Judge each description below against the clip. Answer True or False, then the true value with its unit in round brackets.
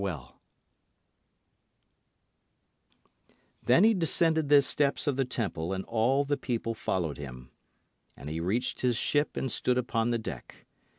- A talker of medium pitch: False (120 Hz)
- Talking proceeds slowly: True (130 wpm)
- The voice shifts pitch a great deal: True (6.9 semitones)